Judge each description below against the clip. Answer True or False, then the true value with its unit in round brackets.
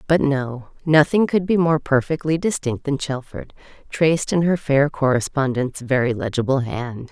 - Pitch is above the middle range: False (140 Hz)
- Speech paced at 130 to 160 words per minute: True (150 wpm)